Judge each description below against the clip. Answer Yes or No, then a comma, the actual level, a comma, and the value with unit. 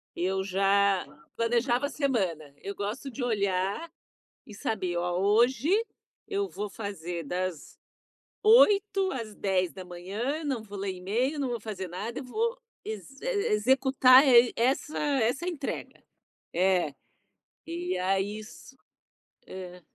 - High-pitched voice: Yes, high, 215 Hz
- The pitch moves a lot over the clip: Yes, wide, 6.1 semitones